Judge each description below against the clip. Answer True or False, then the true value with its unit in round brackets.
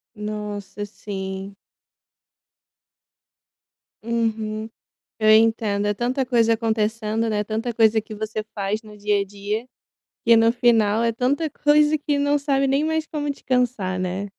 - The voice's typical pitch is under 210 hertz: False (220 Hz)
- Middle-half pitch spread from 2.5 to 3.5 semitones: True (2.9 semitones)